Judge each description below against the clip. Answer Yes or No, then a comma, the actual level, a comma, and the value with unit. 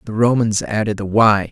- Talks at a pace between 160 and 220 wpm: Yes, average, 200 wpm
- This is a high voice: No, low, 110 Hz